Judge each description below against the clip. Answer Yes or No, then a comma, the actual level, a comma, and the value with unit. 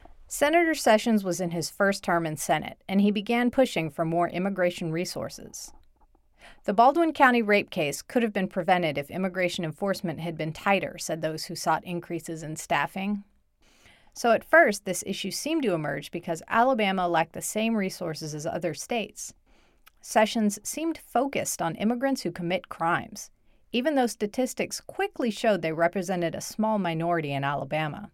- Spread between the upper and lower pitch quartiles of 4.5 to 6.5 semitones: Yes, average, 5.1 semitones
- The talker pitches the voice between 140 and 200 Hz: Yes, high, 190 Hz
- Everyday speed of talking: Yes, average, 160 wpm